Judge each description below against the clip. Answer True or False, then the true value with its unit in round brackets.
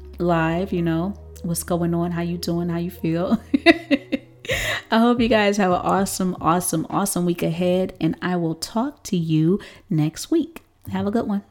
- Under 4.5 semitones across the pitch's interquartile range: True (3.5 semitones)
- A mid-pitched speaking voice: True (180 Hz)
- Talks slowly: False (185 wpm)